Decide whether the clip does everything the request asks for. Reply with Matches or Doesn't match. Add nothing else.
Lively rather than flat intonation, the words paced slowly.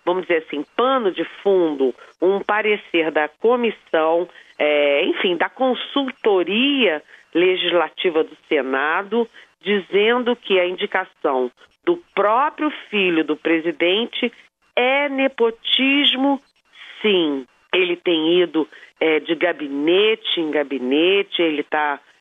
Matches